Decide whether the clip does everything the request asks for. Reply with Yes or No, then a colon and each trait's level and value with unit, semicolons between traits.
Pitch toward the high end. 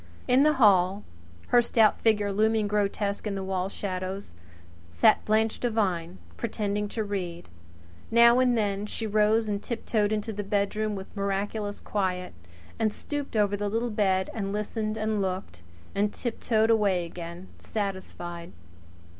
Yes: high, 205 Hz